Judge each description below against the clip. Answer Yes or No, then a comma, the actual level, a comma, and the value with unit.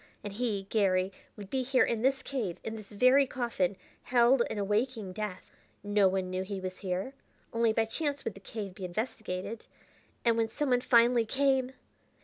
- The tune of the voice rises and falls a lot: No, average, 4.3 semitones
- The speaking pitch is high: Yes, high, 220 Hz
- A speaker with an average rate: Yes, average, 180 wpm